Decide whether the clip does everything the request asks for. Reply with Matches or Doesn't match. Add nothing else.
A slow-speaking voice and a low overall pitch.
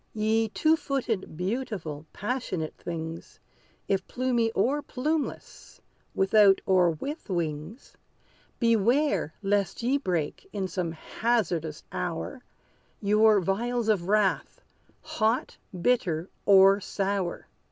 Doesn't match